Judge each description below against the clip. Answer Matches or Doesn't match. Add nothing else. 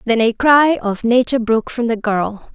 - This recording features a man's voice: Doesn't match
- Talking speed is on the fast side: Matches